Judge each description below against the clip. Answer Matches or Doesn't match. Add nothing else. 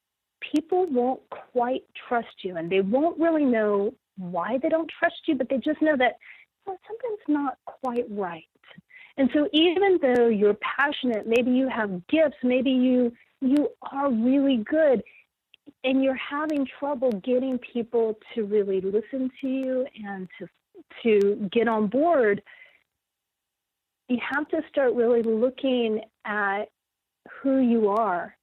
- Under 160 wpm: Matches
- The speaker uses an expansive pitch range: Doesn't match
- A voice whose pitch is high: Matches